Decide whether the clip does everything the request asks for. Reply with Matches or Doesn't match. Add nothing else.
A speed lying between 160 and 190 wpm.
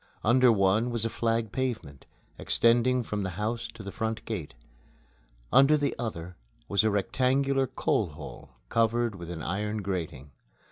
Doesn't match